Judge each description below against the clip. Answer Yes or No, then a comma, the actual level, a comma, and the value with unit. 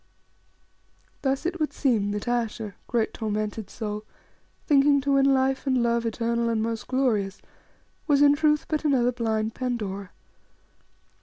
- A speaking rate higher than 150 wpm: No, average, 140 wpm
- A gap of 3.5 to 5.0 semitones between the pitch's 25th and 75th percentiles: Yes, average, 3.9 semitones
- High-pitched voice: Yes, high, 235 Hz